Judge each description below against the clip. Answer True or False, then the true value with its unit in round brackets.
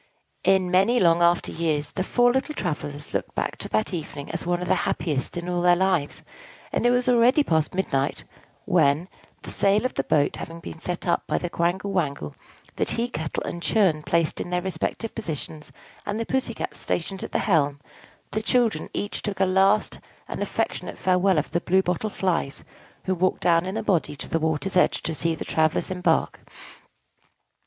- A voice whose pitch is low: False (180 Hz)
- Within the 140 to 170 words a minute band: False (195 wpm)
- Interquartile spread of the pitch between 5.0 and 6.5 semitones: False (3.5 semitones)